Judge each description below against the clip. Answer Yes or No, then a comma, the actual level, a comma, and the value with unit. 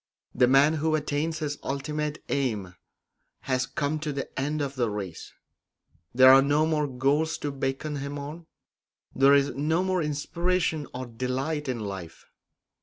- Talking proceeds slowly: No, average, 155 wpm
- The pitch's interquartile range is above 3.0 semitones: No, average, 2.7 semitones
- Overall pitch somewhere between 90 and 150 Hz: Yes, medium, 140 Hz